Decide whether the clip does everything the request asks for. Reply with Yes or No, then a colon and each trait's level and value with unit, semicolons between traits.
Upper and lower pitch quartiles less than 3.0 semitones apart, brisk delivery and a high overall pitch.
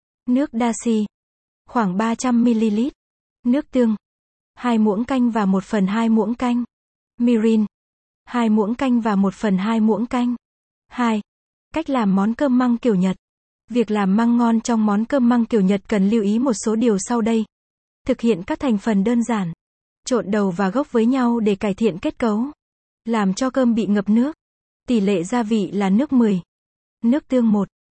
No: narrow, 2.4 semitones; average, 185 wpm; high, 230 Hz